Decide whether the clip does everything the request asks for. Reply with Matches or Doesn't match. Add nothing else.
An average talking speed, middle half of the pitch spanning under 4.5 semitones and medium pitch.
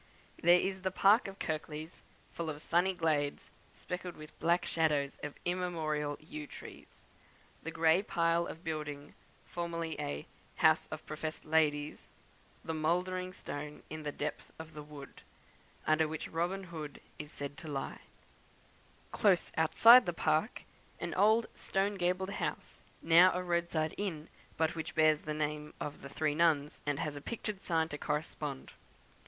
Matches